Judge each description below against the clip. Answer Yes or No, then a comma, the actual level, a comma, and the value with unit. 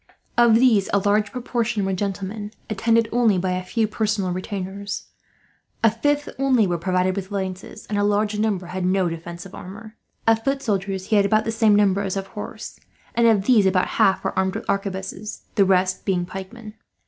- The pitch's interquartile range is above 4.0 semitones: No, average, 2.8 semitones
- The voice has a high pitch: Yes, high, 200 Hz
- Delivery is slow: No, average, 190 wpm